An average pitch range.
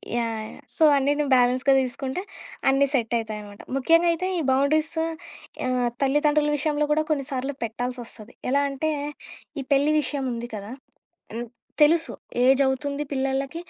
Yes: average, 3.2 semitones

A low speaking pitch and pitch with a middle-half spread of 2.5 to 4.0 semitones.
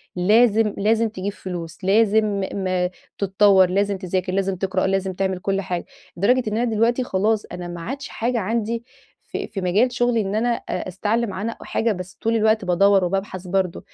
No: high, 200 Hz; average, 3.1 semitones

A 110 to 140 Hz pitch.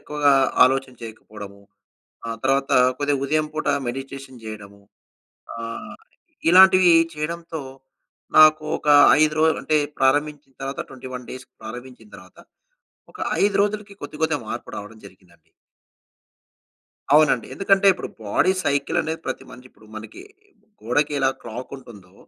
Yes: low, 135 Hz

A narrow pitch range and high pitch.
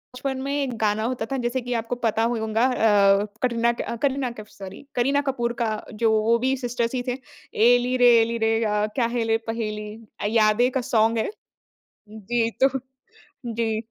Yes: narrow, 2.1 semitones; high, 235 Hz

